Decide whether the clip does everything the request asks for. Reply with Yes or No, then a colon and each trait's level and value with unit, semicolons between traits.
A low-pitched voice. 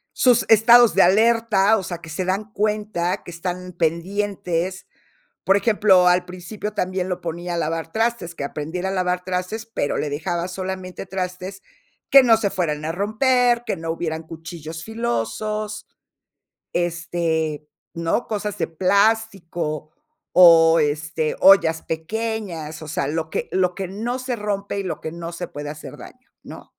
No: medium, 180 Hz